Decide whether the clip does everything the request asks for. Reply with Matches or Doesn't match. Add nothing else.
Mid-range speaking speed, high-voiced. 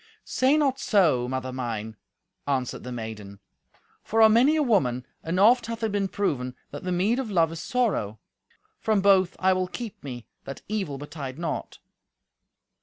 Doesn't match